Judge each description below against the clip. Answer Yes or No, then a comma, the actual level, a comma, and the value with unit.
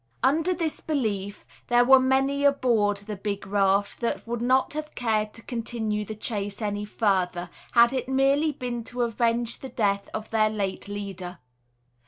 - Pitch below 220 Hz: No, high, 225 Hz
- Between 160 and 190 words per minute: Yes, average, 165 wpm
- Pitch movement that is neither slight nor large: Yes, average, 4.0 semitones